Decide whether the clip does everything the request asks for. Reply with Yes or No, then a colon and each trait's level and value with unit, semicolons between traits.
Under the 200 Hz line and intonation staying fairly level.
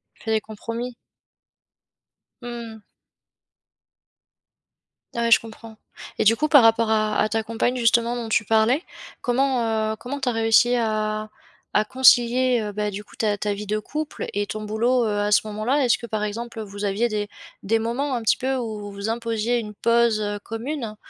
No: high, 225 Hz; narrow, 2.1 semitones